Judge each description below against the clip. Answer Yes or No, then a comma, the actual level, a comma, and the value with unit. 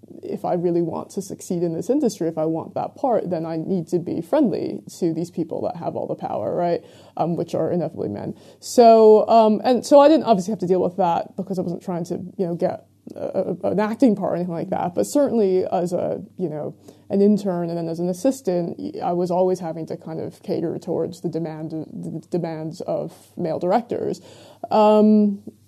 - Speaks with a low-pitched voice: No, medium, 185 Hz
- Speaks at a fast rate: Yes, fast, 215 wpm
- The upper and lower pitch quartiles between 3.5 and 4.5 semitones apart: Yes, average, 3.9 semitones